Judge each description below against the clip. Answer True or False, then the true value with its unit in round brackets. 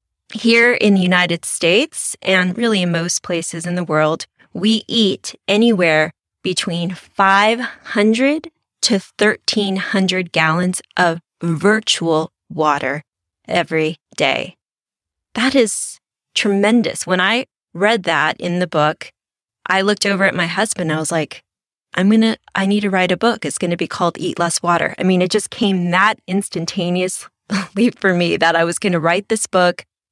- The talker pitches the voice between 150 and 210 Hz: True (185 Hz)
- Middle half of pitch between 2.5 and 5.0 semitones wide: True (3.6 semitones)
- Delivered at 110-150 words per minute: False (160 wpm)